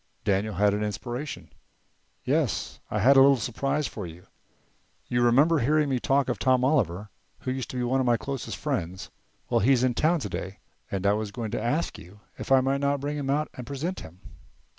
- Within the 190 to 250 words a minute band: Yes, fast, 205 wpm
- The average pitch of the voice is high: No, low, 125 Hz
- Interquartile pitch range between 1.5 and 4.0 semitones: No, average, 4.9 semitones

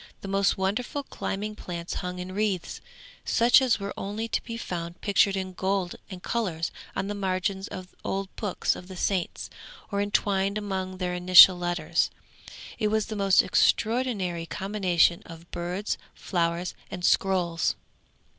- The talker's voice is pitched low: No, high, 190 Hz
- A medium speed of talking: Yes, average, 150 wpm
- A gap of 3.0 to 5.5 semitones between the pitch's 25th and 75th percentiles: No, narrow, 2.4 semitones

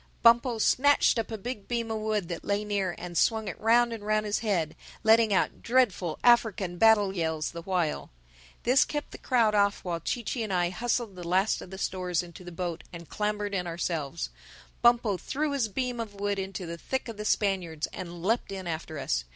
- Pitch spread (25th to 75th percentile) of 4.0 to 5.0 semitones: Yes, average, 4.3 semitones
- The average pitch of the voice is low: No, high, 200 Hz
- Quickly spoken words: Yes, fast, 210 wpm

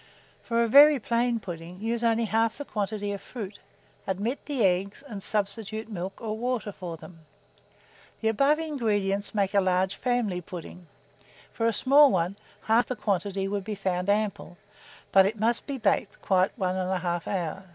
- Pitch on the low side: No, high, 205 Hz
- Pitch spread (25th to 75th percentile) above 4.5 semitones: No, average, 3.5 semitones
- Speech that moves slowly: No, average, 170 wpm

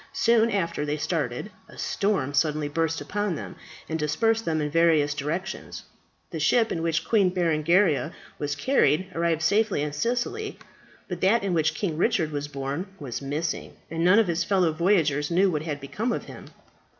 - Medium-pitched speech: Yes, medium, 165 Hz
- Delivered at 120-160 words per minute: No, average, 175 wpm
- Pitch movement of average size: Yes, average, 4.7 semitones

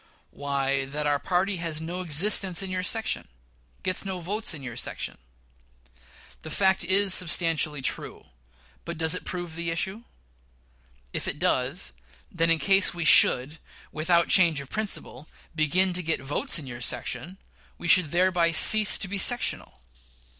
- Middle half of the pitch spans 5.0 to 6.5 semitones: No, average, 3.8 semitones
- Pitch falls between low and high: Yes, medium, 170 Hz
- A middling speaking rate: Yes, average, 155 wpm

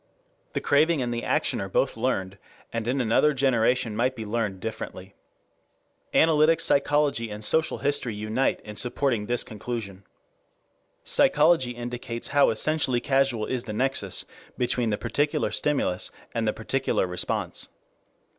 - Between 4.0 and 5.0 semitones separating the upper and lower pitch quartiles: Yes, average, 4.3 semitones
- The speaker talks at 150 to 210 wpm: No, slow, 135 wpm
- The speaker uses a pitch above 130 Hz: No, low, 120 Hz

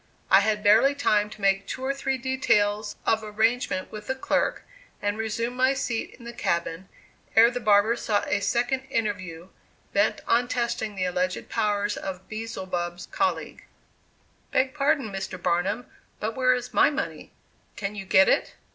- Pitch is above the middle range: Yes, high, 215 Hz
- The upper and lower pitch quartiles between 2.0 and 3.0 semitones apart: No, average, 3.8 semitones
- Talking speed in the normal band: Yes, average, 165 wpm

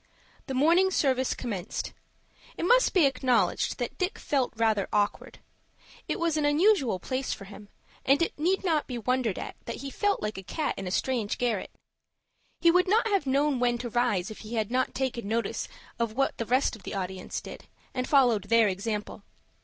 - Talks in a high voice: Yes, very high, 250 Hz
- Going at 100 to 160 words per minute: No, average, 195 wpm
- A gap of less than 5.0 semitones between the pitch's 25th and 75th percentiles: No, average, 5.3 semitones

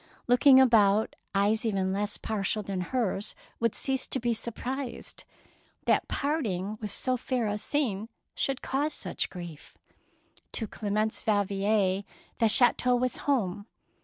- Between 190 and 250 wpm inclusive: No, slow, 135 wpm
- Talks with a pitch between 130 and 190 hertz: No, high, 220 Hz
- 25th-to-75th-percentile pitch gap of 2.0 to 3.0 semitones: No, average, 3.9 semitones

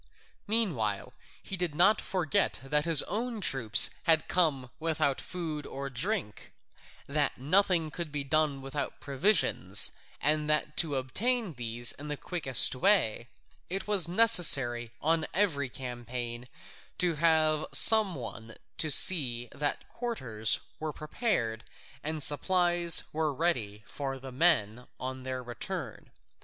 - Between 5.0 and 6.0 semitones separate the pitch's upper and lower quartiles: Yes, wide, 5.4 semitones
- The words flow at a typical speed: No, slow, 125 wpm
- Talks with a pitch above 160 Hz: No, medium, 150 Hz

